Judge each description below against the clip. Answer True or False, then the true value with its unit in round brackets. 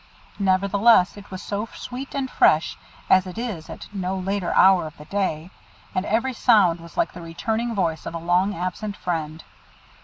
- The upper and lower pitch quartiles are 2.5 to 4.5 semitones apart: True (3.5 semitones)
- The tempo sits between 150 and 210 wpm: True (180 wpm)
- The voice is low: False (190 Hz)